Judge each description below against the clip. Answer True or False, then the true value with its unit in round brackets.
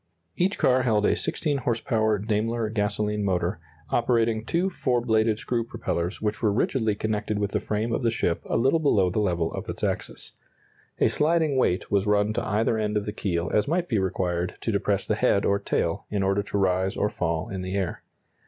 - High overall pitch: False (105 Hz)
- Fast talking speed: True (210 wpm)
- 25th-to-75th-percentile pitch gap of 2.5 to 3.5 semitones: True (3.0 semitones)